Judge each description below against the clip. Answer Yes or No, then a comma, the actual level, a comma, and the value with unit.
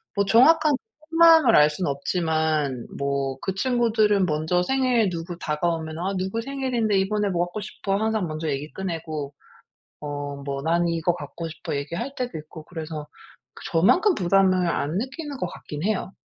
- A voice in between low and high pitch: Yes, medium, 180 Hz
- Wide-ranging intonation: Yes, wide, 5.8 semitones